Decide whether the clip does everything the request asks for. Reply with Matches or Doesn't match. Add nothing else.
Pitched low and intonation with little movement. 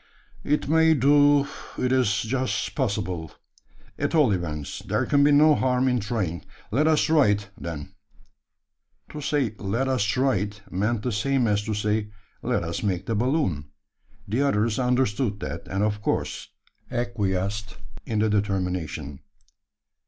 Doesn't match